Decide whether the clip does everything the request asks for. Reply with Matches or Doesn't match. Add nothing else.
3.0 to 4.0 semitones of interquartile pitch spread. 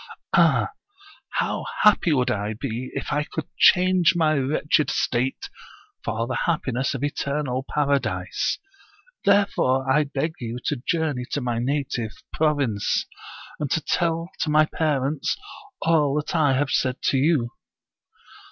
Matches